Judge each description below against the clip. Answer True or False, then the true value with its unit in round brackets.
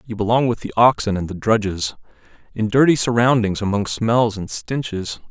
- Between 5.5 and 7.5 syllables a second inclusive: False (5.1 syllables/s)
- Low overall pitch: True (110 Hz)